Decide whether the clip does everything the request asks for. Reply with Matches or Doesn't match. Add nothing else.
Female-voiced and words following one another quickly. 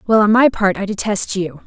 Matches